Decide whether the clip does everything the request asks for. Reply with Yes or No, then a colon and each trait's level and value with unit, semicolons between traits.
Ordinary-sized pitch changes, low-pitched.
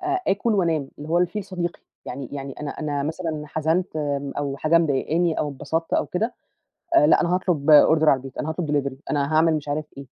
No: average, 3.2 semitones; medium, 155 Hz